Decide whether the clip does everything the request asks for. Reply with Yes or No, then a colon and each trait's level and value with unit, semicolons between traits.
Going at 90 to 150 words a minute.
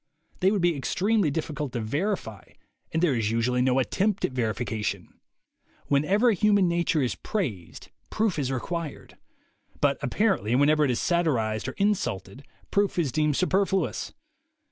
Yes: average, 145 wpm